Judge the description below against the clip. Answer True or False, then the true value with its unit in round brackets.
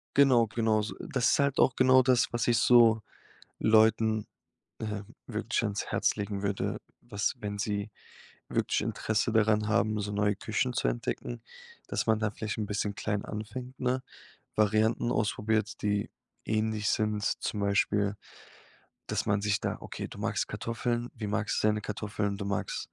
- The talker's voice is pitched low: True (110 Hz)